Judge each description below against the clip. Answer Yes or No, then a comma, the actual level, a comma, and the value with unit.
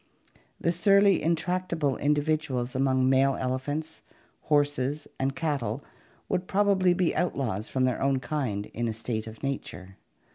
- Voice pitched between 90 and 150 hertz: Yes, medium, 140 Hz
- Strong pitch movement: No, average, 4.2 semitones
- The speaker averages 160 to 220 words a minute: No, slow, 135 wpm